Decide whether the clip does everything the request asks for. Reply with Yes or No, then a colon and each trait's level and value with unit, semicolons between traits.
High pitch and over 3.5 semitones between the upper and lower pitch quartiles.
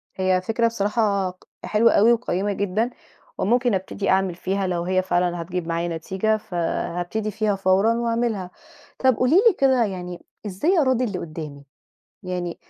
Yes: high, 195 Hz; average, 4.1 semitones